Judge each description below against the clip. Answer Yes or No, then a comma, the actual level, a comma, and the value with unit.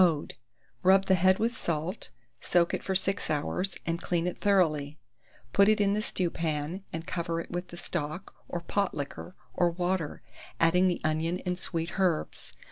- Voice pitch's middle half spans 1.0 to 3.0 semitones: Yes, narrow, 2.4 semitones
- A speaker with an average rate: Yes, average, 175 wpm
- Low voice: No, medium, 175 Hz